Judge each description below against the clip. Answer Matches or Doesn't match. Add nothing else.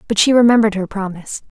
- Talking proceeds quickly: Doesn't match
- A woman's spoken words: Matches